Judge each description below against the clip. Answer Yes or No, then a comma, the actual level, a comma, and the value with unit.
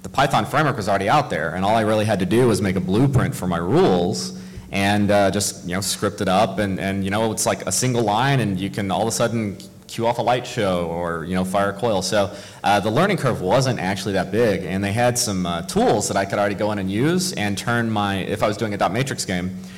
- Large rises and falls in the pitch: No, average, 3.0 semitones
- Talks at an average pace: No, fast, 275 wpm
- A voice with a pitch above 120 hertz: No, low, 100 Hz